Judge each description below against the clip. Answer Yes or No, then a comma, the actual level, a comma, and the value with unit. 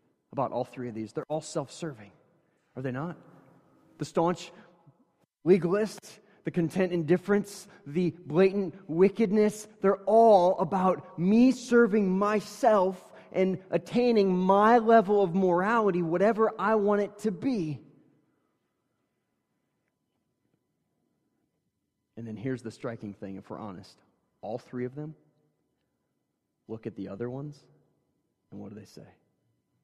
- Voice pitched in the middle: Yes, medium, 180 Hz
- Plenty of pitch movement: Yes, wide, 6.5 semitones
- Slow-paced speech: Yes, slow, 125 wpm